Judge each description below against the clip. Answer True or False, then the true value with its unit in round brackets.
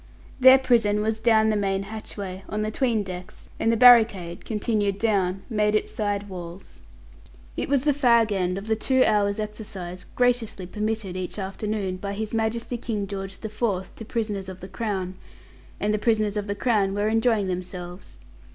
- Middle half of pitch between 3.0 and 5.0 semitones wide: False (2.5 semitones)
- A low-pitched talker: False (210 Hz)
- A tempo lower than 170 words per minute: False (180 wpm)